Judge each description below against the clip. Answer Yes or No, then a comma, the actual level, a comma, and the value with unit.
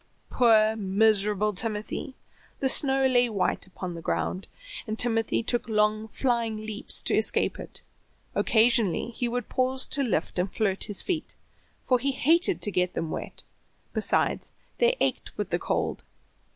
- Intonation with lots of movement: No, average, 3.4 semitones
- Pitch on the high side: Yes, high, 220 Hz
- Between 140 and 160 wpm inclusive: Yes, average, 150 wpm